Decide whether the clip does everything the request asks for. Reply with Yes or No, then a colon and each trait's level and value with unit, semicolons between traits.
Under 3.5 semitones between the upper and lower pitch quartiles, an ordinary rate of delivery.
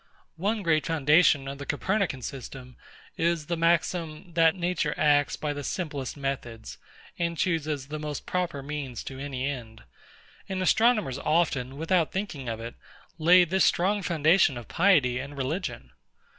No: average, 4.2 semitones; average, 150 wpm